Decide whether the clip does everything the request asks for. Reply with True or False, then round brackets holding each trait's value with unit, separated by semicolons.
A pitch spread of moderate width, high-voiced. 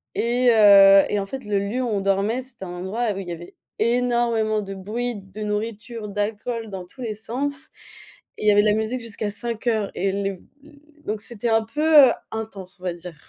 True (3.2 semitones; 215 Hz)